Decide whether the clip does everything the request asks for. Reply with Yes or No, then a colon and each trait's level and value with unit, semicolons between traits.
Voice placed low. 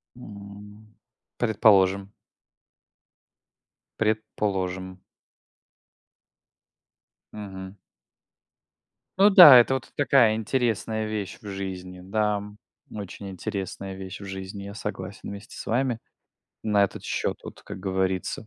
Yes: low, 100 Hz